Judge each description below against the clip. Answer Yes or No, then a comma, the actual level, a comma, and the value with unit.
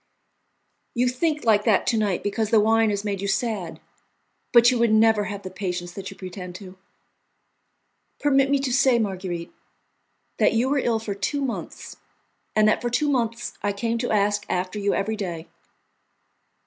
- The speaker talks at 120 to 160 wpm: No, average, 175 wpm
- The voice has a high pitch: Yes, high, 215 Hz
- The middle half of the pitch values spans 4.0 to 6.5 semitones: No, average, 3.3 semitones